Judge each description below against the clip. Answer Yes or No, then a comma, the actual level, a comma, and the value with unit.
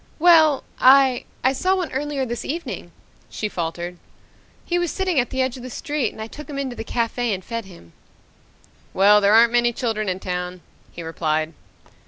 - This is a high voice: Yes, high, 240 Hz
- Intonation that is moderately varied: No, wide, 6.5 semitones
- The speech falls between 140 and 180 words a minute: No, average, 190 wpm